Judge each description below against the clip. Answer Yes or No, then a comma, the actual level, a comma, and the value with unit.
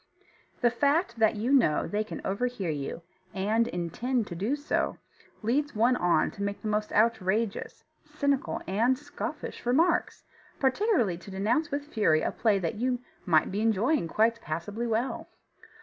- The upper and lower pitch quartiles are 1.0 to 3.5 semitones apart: No, average, 4.4 semitones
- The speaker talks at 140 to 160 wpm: Yes, average, 155 wpm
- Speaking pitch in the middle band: No, high, 225 Hz